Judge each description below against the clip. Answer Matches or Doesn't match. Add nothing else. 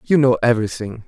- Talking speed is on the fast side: Doesn't match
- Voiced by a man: Matches